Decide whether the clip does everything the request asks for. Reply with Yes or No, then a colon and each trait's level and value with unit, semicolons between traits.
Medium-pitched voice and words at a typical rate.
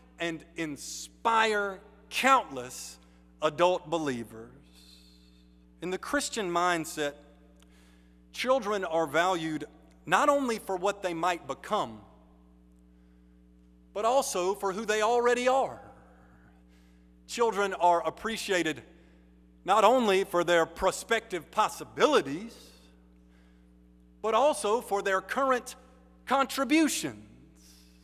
No: medium, 160 Hz; slow, 90 wpm